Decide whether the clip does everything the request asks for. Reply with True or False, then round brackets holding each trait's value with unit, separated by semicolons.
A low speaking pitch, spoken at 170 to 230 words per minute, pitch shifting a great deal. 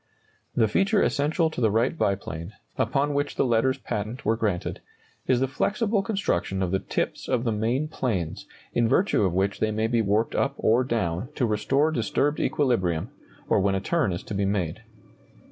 True (115 Hz; 185 wpm; 5.8 semitones)